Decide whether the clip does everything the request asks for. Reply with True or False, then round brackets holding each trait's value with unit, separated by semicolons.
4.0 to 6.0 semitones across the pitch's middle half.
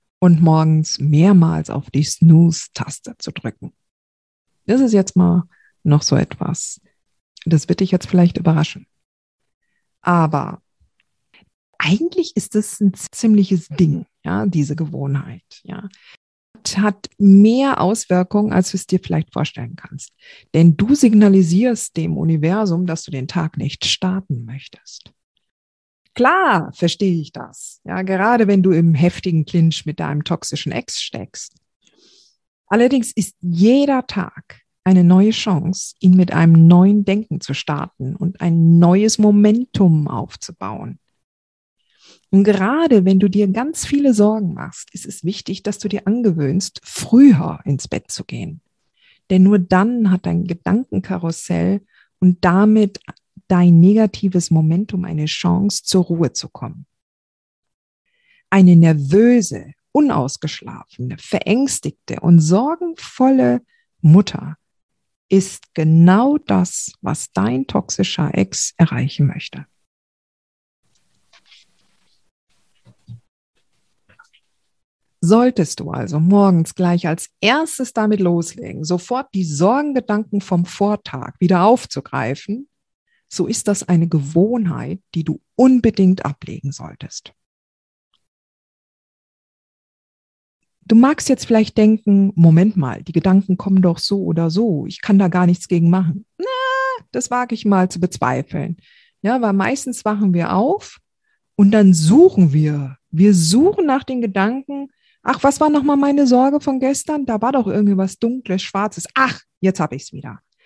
True (4.5 semitones)